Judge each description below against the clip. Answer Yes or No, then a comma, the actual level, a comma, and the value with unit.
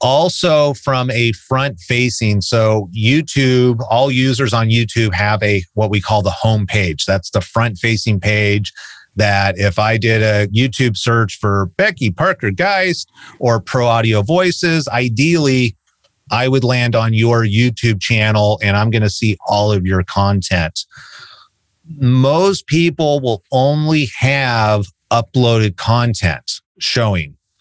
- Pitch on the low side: Yes, low, 115 Hz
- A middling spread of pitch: Yes, average, 3.6 semitones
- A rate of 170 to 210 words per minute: No, average, 140 wpm